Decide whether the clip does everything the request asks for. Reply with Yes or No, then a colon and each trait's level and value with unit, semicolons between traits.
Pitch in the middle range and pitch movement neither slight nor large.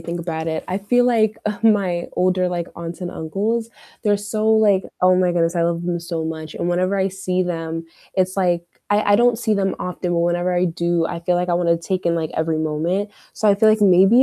Yes: medium, 180 Hz; average, 3.1 semitones